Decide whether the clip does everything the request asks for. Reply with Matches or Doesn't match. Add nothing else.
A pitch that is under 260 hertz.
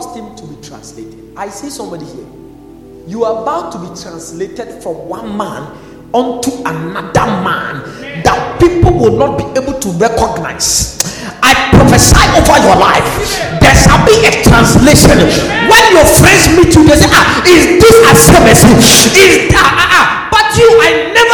Doesn't match